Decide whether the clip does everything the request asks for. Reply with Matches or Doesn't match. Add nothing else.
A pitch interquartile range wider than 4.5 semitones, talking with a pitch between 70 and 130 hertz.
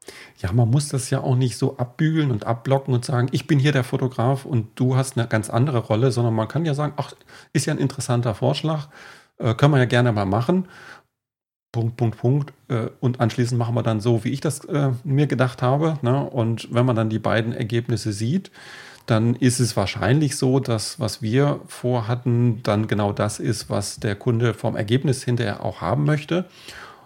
Doesn't match